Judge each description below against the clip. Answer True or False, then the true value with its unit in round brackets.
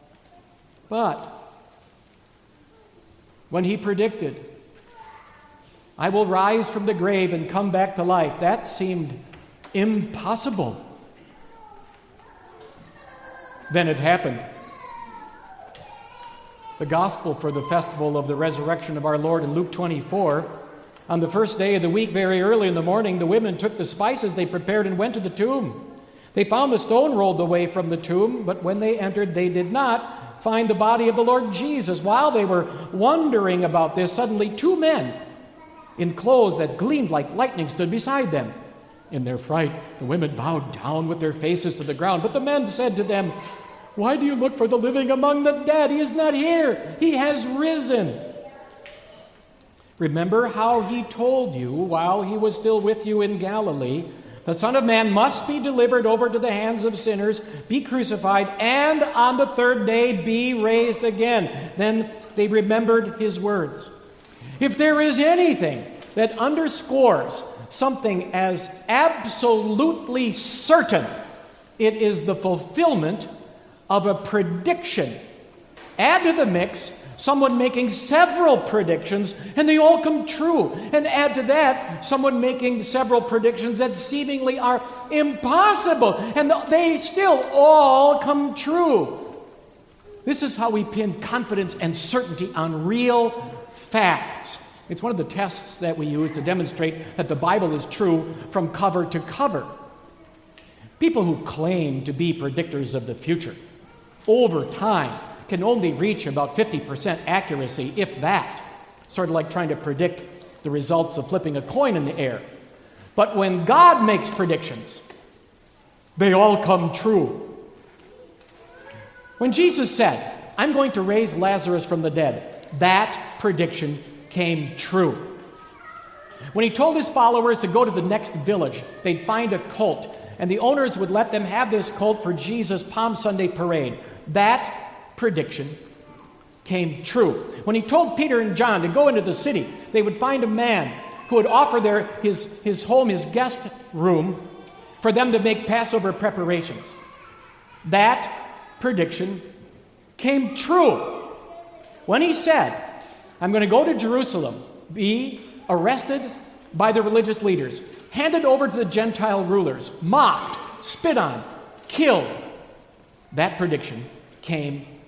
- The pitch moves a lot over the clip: True (6.4 semitones)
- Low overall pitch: False (210 Hz)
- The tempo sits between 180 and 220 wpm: False (150 wpm)